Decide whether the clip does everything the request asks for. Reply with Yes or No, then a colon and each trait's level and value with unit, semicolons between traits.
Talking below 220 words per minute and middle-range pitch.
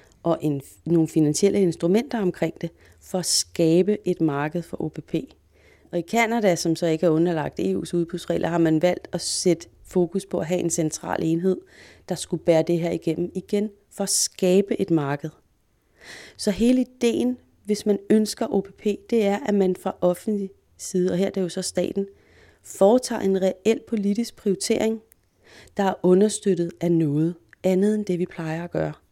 Yes: average, 175 wpm; medium, 180 Hz